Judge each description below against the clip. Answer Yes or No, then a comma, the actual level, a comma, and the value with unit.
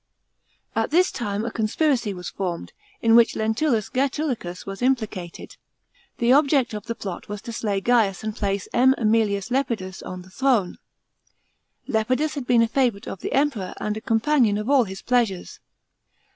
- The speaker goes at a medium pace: Yes, average, 170 wpm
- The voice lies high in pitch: Yes, high, 225 Hz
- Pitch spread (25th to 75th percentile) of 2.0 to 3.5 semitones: No, average, 4.2 semitones